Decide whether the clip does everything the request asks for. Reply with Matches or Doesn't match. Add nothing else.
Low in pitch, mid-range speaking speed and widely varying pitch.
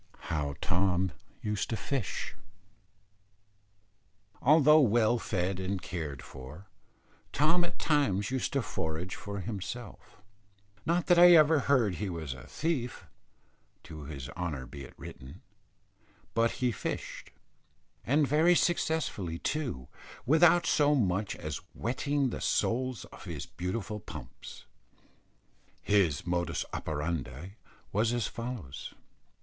Doesn't match